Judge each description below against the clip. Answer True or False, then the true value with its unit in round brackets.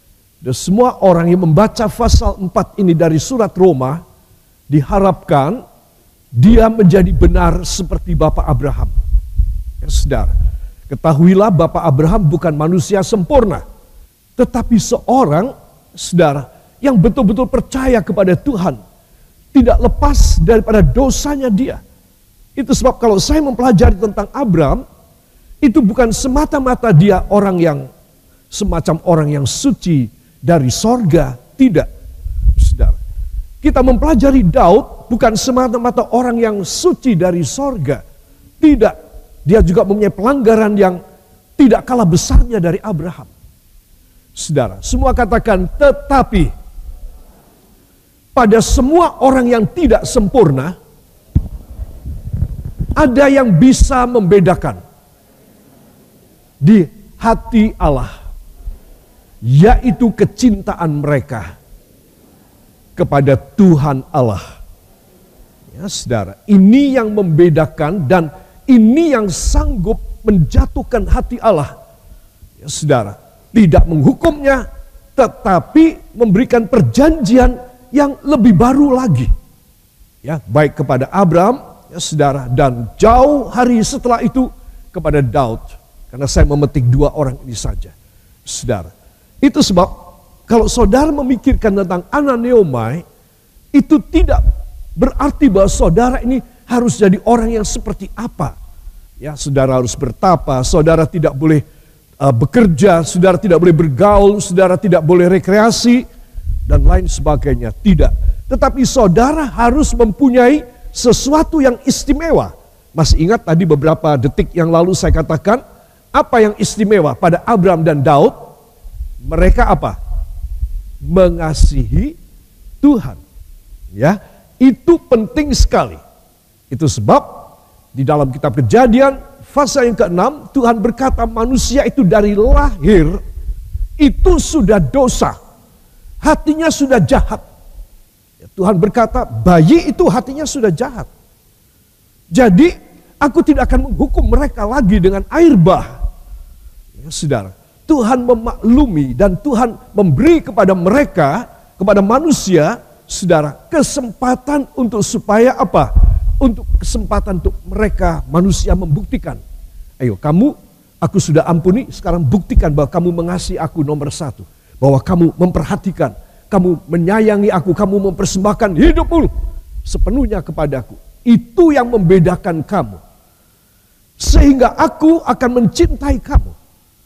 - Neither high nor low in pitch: False (195 Hz)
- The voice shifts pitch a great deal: True (8.7 semitones)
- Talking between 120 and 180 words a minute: False (105 wpm)